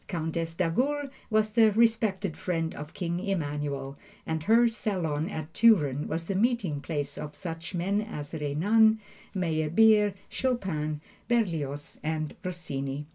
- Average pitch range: No, wide, 6.0 semitones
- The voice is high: No, medium, 170 Hz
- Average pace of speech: No, slow, 130 wpm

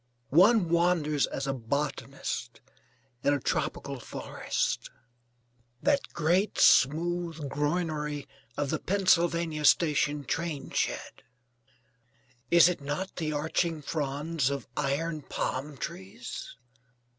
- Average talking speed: No, slow, 100 wpm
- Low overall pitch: No, medium, 150 Hz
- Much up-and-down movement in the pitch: No, average, 3.3 semitones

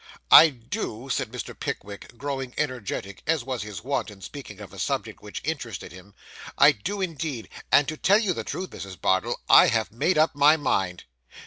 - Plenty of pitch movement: Yes, wide, 7.0 semitones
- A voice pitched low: Yes, low, 130 Hz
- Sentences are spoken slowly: No, average, 190 wpm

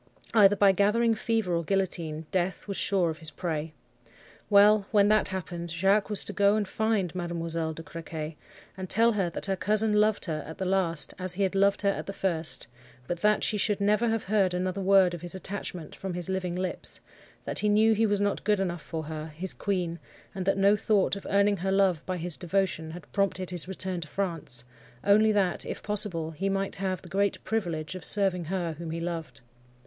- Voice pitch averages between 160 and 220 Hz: Yes, high, 190 Hz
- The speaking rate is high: Yes, fast, 210 wpm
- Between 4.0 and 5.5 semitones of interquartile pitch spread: No, average, 2.8 semitones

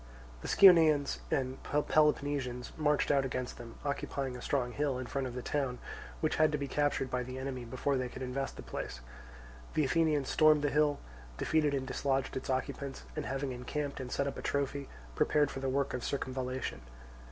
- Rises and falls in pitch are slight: Yes, narrow, 2.2 semitones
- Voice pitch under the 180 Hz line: Yes, low, 135 Hz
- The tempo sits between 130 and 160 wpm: No, average, 190 wpm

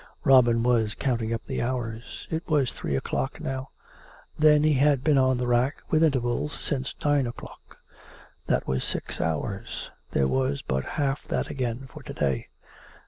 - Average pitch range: Yes, average, 3.4 semitones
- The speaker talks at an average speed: Yes, average, 165 wpm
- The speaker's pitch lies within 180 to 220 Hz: No, low, 130 Hz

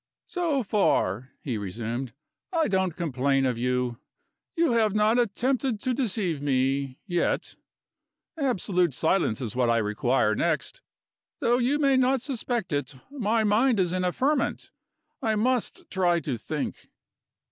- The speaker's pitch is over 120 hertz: Yes, medium, 185 Hz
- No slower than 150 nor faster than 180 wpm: No, average, 140 wpm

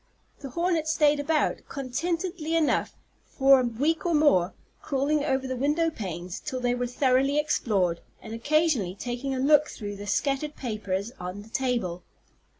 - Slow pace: No, average, 155 wpm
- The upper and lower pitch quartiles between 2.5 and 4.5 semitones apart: No, average, 5.3 semitones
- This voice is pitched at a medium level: No, very high, 265 Hz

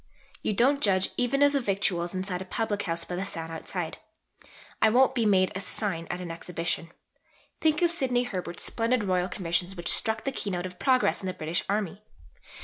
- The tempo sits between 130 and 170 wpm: No, average, 195 wpm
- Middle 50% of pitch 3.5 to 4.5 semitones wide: No, average, 5.1 semitones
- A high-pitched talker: Yes, high, 195 Hz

